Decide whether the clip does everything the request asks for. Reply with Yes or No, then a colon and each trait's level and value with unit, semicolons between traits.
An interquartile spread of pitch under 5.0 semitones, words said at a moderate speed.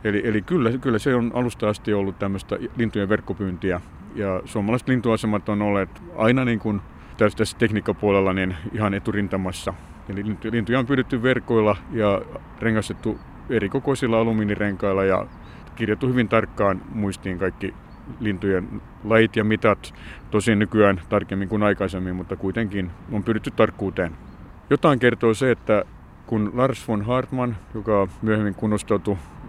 Yes: average, 2.8 semitones; average, 135 wpm